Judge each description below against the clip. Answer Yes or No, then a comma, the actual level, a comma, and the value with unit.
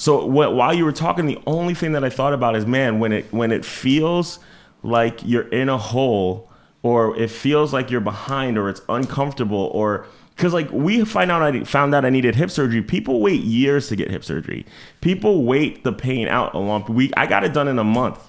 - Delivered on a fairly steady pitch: No, average, 4.3 semitones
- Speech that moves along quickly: Yes, fast, 225 wpm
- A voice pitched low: Yes, low, 130 Hz